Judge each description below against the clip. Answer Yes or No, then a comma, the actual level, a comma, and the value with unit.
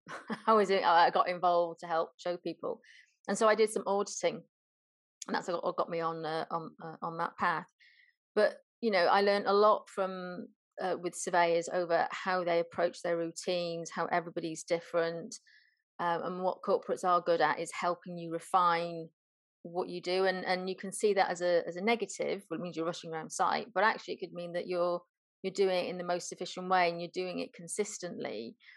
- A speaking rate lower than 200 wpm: No, fast, 205 wpm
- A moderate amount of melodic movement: No, narrow, 2.3 semitones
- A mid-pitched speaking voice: Yes, medium, 175 Hz